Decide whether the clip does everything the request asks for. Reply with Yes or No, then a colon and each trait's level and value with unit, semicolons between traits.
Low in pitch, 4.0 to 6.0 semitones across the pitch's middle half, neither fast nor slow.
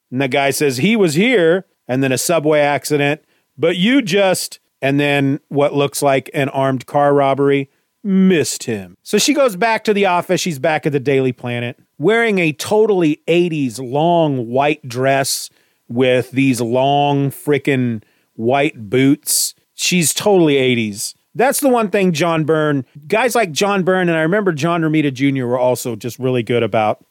No: medium, 145 Hz; average, 4.9 semitones; average, 170 wpm